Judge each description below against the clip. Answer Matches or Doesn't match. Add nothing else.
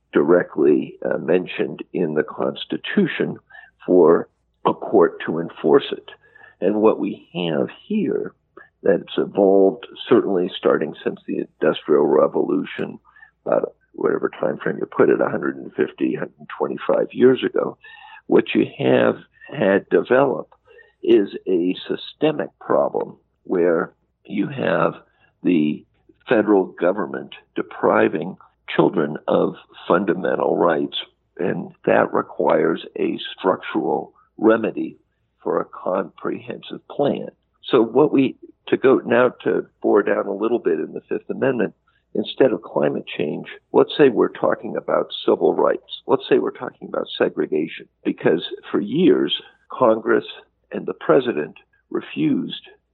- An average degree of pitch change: Matches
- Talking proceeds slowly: Matches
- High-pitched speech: Matches